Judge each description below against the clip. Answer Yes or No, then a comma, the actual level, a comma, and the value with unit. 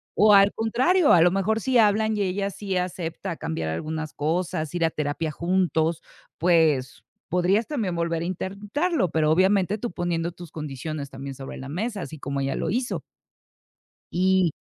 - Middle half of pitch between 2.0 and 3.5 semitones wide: No, average, 4.2 semitones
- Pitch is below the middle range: No, medium, 175 Hz